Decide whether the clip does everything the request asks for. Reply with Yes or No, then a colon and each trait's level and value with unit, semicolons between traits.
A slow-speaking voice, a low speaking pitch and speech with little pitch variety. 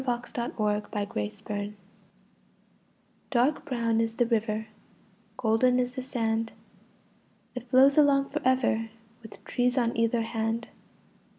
No: slow, 130 wpm; high, 235 Hz; narrow, 2.2 semitones